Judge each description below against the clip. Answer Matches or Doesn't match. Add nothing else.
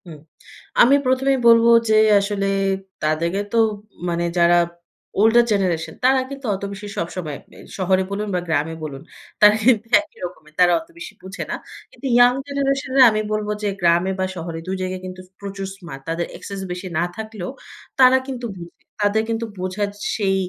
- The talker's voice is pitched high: Matches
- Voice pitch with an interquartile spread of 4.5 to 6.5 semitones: Matches